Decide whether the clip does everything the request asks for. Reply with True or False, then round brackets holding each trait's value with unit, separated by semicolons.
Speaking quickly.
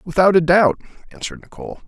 False (160 wpm)